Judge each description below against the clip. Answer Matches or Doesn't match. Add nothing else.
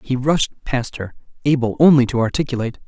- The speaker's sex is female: Doesn't match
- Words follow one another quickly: Doesn't match